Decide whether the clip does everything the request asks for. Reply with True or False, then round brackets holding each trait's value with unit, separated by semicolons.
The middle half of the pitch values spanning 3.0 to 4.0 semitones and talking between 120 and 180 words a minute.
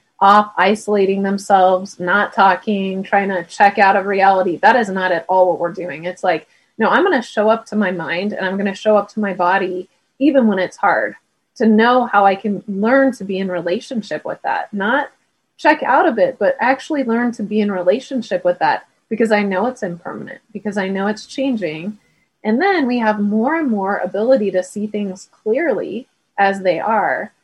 False (3.3 semitones; 205 wpm)